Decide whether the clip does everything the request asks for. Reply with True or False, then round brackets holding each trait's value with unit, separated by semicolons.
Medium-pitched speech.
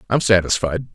False (100 Hz)